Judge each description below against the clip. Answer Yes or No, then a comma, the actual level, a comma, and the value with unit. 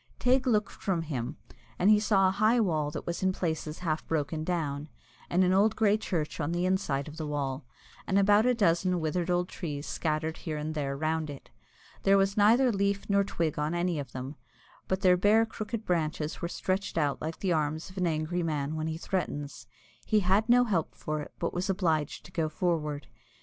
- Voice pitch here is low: No, medium, 170 Hz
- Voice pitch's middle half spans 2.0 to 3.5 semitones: No, average, 4.2 semitones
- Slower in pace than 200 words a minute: No, fast, 205 wpm